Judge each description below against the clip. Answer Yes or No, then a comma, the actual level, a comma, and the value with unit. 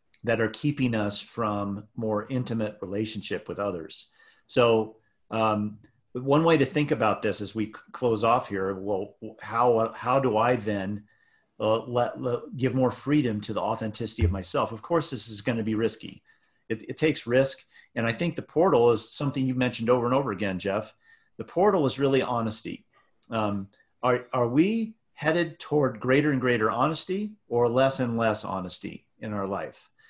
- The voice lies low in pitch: Yes, low, 120 Hz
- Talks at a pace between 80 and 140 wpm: No, average, 180 wpm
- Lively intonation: No, average, 3.7 semitones